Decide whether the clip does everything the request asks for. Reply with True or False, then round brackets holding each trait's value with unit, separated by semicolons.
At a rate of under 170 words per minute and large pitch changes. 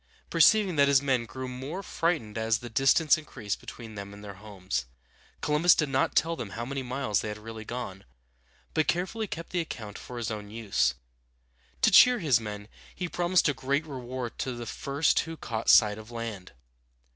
False (190 wpm; 5.7 semitones)